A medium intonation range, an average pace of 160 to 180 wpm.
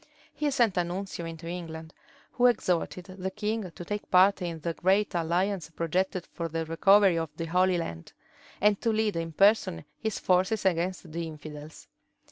Yes: average, 3.2 semitones; average, 170 wpm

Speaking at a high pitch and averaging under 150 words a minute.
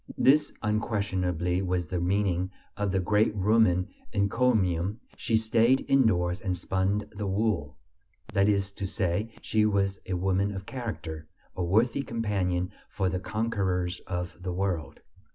No: low, 100 Hz; average, 140 wpm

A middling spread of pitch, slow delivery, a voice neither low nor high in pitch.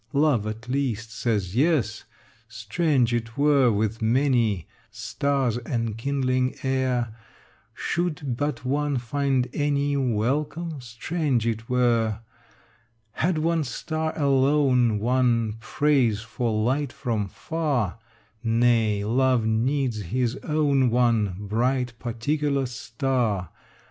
No: average, 3.8 semitones; slow, 105 wpm; low, 125 Hz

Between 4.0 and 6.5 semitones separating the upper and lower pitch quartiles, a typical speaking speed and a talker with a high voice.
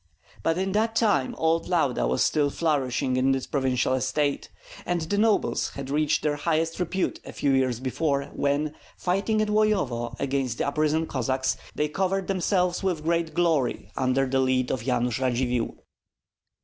No: average, 5.0 semitones; average, 160 wpm; medium, 145 Hz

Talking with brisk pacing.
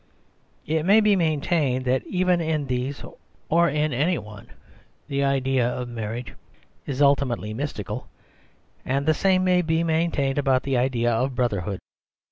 No: average, 150 wpm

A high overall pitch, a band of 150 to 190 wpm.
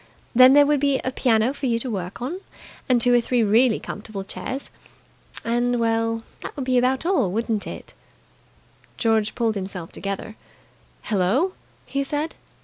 Yes: high, 235 Hz; average, 160 wpm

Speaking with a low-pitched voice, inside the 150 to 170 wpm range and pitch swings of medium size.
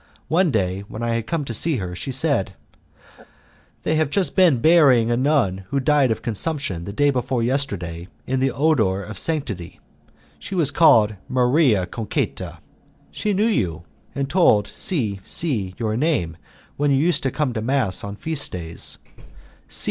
No: low, 130 Hz; average, 165 wpm; wide, 6.6 semitones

